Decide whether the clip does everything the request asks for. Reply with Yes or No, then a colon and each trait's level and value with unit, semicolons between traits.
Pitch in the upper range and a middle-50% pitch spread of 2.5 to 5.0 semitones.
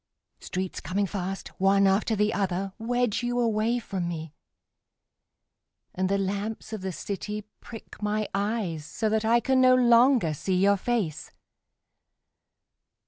Yes: high, 205 Hz; average, 3.1 semitones